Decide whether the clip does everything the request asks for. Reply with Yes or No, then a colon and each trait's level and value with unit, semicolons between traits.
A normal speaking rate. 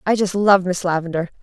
No: fast, 210 wpm